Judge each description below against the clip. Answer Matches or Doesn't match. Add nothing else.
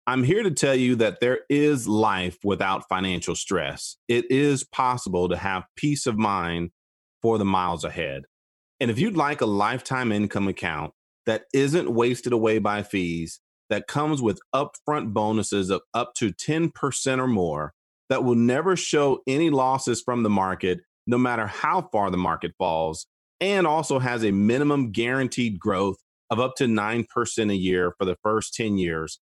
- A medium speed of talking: Matches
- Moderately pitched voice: Doesn't match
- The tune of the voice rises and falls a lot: Matches